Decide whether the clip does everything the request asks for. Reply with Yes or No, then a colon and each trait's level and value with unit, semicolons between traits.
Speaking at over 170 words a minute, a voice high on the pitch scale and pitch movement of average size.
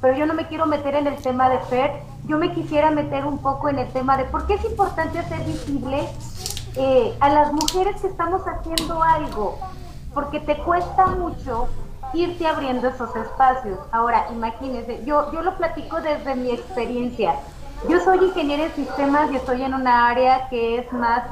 Yes: average, 185 wpm; very high, 290 Hz; average, 4.2 semitones